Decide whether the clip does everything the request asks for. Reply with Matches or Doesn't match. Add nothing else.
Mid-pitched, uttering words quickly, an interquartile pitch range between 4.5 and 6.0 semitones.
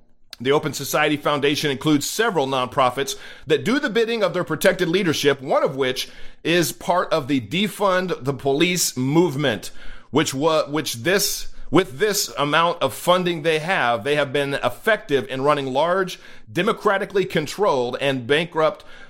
Doesn't match